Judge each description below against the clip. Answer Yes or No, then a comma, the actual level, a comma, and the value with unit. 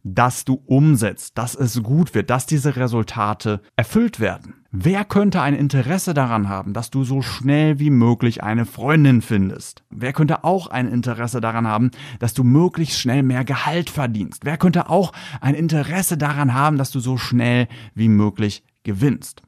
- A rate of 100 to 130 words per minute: No, average, 170 wpm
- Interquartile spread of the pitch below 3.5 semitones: No, average, 4.2 semitones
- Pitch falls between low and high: No, low, 130 Hz